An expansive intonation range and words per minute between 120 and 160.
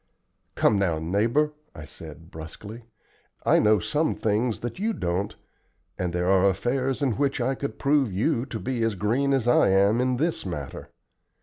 No: wide, 6.0 semitones; average, 175 wpm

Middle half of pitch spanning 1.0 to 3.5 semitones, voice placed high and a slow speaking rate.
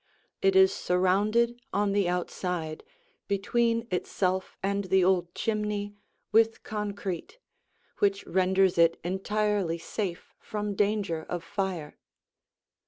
Yes: average, 2.8 semitones; high, 200 Hz; slow, 105 wpm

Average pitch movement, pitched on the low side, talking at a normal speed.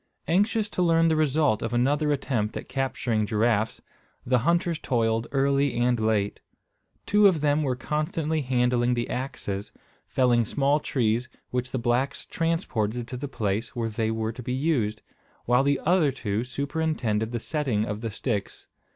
Yes: average, 4.7 semitones; low, 125 Hz; average, 160 wpm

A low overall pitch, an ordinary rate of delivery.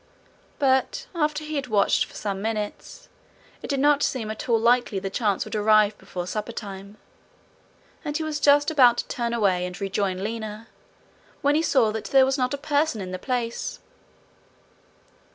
No: high, 230 Hz; average, 170 wpm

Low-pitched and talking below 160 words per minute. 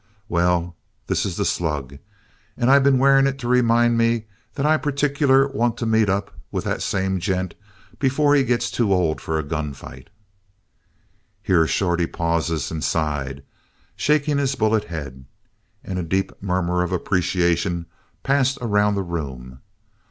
Yes: very low, 95 Hz; average, 150 wpm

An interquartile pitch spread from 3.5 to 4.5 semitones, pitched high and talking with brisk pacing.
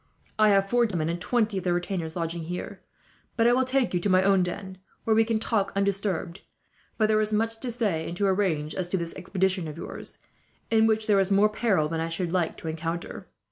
Yes: average, 3.9 semitones; high, 195 Hz; fast, 230 wpm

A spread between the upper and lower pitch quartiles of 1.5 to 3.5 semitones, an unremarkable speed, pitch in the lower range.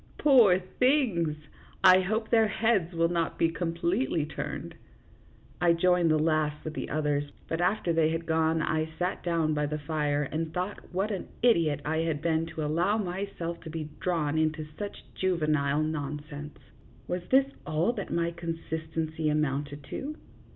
No: average, 2.8 semitones; average, 160 wpm; medium, 165 Hz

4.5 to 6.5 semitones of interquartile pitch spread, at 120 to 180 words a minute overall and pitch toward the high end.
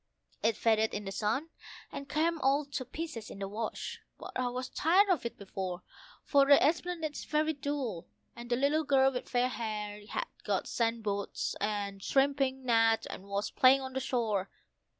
No: average, 4.9 semitones; average, 190 wpm; very high, 250 Hz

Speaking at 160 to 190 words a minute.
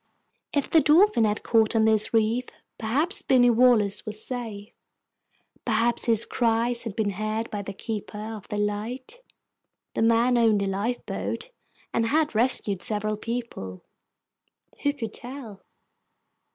No: average, 140 wpm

